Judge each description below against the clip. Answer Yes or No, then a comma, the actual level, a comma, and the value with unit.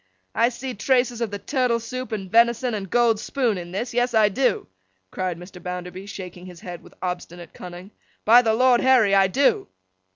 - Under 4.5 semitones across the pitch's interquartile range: No, average, 4.9 semitones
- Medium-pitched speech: No, high, 220 Hz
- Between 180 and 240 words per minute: Yes, average, 190 wpm